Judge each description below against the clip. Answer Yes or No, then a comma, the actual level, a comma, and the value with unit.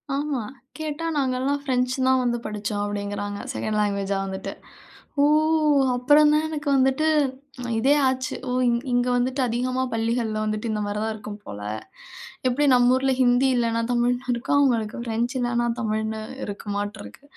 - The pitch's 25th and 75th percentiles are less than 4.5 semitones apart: Yes, average, 3.4 semitones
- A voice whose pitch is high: Yes, high, 240 Hz